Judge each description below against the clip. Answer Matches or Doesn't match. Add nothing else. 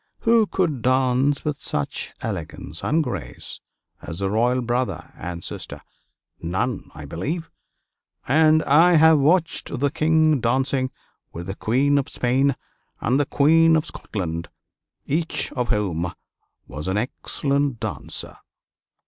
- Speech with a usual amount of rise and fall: Doesn't match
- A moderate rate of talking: Doesn't match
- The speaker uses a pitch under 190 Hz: Matches